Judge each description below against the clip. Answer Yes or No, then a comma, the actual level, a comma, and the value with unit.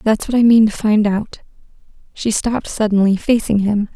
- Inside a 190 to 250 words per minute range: No, average, 180 wpm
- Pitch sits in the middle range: No, high, 215 Hz